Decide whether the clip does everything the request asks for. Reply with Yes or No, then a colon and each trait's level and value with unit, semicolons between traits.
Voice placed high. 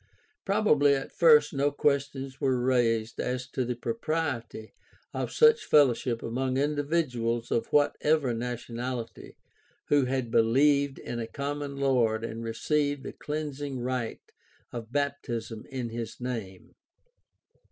No: low, 130 Hz